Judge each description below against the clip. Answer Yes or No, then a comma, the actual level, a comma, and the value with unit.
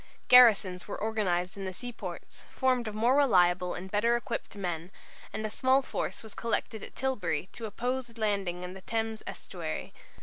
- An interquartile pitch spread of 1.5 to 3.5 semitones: No, average, 4.3 semitones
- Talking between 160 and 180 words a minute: Yes, average, 175 wpm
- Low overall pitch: No, high, 215 Hz